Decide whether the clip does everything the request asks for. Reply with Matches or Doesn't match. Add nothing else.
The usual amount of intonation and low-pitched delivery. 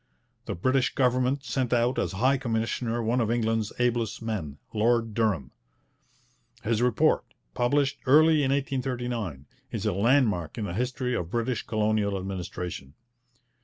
Matches